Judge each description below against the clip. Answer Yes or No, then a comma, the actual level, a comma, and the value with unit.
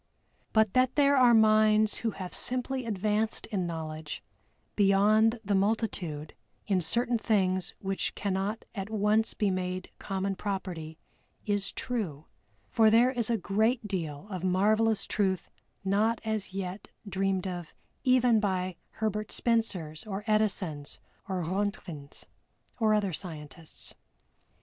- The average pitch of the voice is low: No, high, 200 Hz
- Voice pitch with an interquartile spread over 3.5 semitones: No, average, 3.0 semitones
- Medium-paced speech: No, slow, 125 wpm